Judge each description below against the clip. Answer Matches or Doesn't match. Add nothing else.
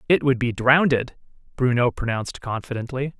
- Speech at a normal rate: Doesn't match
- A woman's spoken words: Doesn't match